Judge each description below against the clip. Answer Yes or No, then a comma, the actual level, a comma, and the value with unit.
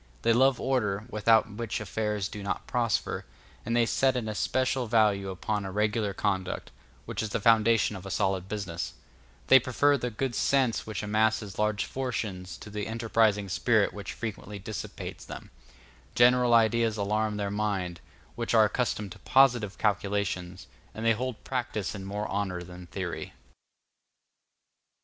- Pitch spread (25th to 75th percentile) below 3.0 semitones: Yes, narrow, 2.6 semitones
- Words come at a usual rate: Yes, average, 155 wpm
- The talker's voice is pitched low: Yes, low, 105 Hz